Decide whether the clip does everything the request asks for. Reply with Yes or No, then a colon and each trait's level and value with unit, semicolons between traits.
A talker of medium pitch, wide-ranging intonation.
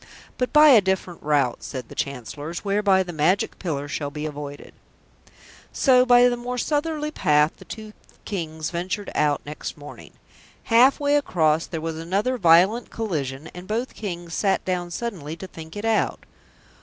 Yes: medium, 180 Hz; wide, 6.6 semitones